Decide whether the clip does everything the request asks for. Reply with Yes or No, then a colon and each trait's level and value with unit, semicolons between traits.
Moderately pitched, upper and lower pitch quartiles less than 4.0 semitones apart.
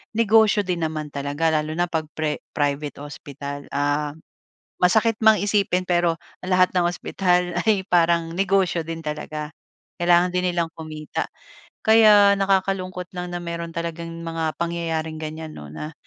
Yes: medium, 170 Hz; average, 2.8 semitones